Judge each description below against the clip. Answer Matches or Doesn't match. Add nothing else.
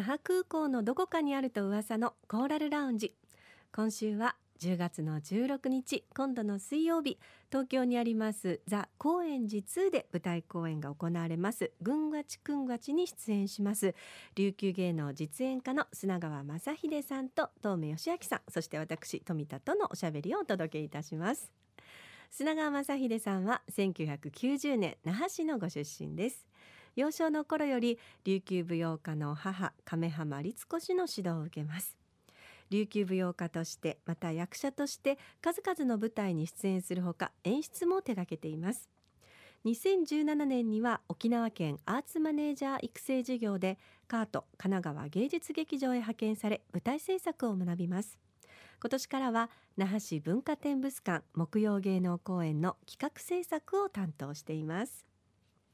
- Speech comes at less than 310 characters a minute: Matches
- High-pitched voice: Matches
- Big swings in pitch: Matches